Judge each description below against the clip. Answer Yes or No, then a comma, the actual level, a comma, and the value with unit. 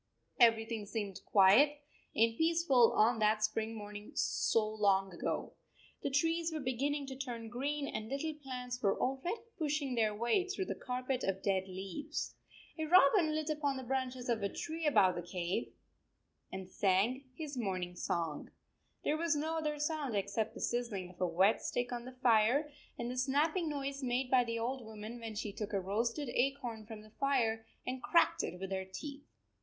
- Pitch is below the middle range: No, high, 245 Hz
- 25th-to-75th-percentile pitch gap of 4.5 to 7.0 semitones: Yes, average, 5.1 semitones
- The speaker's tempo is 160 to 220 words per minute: Yes, average, 180 wpm